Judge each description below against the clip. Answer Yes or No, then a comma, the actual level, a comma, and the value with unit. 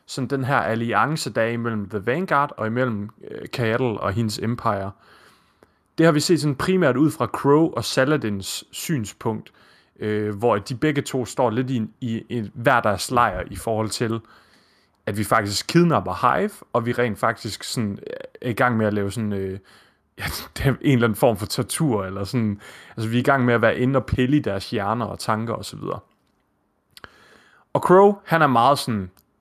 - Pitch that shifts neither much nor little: Yes, average, 4.2 semitones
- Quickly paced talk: No, average, 190 wpm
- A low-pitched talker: Yes, low, 115 Hz